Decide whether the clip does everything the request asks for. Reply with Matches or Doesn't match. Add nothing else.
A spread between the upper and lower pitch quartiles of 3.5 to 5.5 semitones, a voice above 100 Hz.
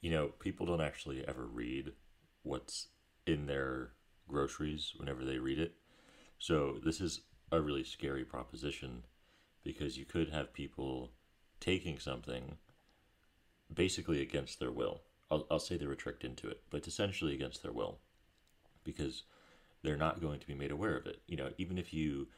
Doesn't match